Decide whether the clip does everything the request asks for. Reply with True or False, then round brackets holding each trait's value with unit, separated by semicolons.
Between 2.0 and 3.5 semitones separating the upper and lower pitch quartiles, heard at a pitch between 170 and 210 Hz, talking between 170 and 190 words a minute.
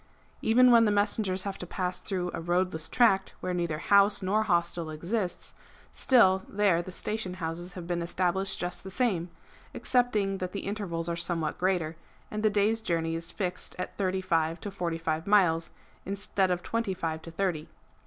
True (3.0 semitones; 185 Hz; 185 wpm)